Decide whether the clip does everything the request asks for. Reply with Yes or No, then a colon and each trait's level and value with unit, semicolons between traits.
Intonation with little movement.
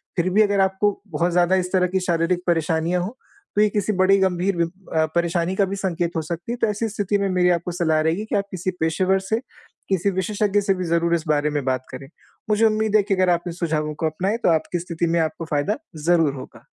No: average, 3.0 semitones